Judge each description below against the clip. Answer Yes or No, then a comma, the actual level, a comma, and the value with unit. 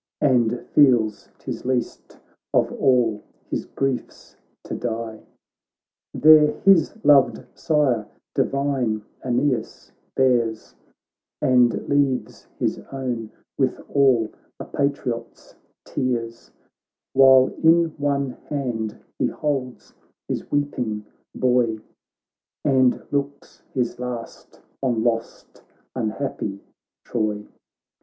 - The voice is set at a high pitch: No, low, 125 Hz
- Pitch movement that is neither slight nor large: Yes, average, 3.3 semitones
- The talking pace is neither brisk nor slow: No, slow, 90 wpm